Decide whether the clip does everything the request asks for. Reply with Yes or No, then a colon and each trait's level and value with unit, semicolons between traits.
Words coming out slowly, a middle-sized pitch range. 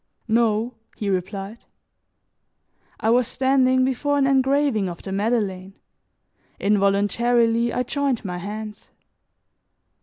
Yes: slow, 100 wpm; average, 4.2 semitones